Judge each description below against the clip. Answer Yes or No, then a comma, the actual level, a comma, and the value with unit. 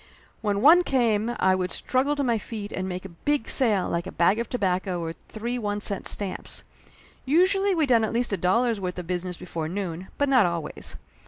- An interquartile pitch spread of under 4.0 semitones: No, average, 5.3 semitones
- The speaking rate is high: Yes, fast, 210 wpm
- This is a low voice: No, high, 205 Hz